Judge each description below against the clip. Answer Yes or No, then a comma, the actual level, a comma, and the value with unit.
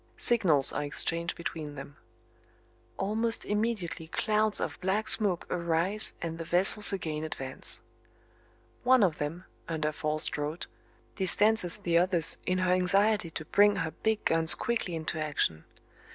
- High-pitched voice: No, medium, 175 Hz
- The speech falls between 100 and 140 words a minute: Yes, slow, 135 wpm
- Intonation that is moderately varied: Yes, average, 4.7 semitones